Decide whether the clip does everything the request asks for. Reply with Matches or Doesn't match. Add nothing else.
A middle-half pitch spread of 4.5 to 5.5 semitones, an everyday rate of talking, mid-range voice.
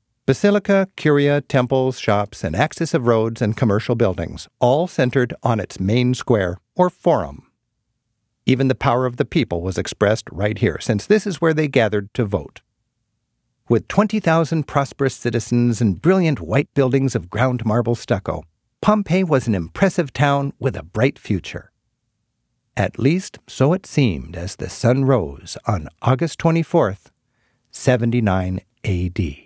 Doesn't match